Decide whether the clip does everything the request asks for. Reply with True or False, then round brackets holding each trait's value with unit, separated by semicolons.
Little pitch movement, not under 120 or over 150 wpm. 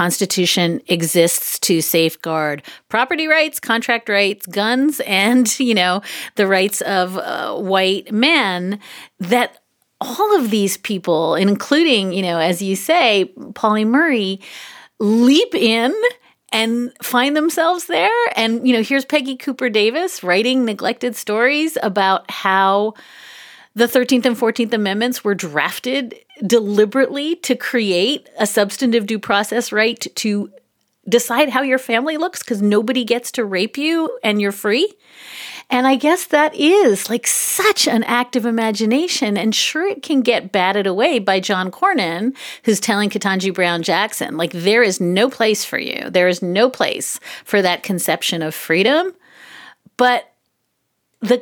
False (5.1 semitones; 145 wpm)